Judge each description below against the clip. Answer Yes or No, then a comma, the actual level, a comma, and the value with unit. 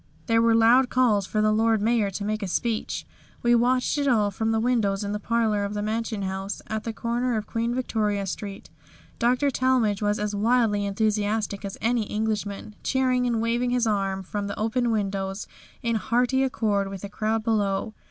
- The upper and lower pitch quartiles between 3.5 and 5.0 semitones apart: No, narrow, 2.5 semitones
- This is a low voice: No, high, 220 Hz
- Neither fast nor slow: Yes, average, 190 wpm